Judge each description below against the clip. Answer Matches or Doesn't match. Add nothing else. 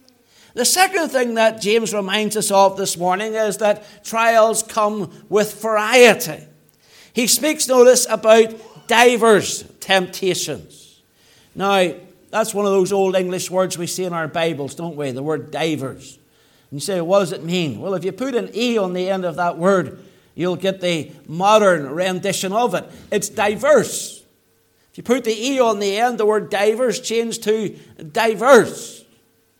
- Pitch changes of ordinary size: Matches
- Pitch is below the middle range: Doesn't match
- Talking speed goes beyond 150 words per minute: Matches